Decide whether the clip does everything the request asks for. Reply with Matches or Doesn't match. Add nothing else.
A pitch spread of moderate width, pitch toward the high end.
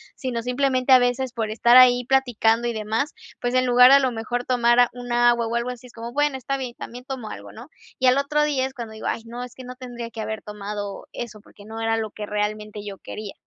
Doesn't match